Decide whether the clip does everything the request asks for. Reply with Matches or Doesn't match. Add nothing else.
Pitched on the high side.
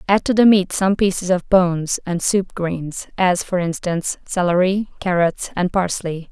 Doesn't match